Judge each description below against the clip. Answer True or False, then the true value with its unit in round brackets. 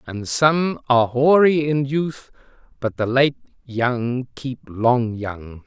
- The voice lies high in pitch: False (130 Hz)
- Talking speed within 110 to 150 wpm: True (140 wpm)